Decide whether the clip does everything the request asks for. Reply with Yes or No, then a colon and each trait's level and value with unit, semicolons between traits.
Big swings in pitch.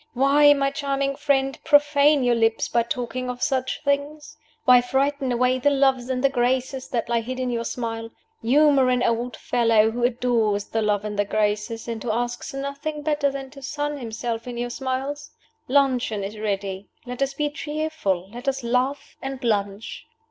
No: average, 3.2 semitones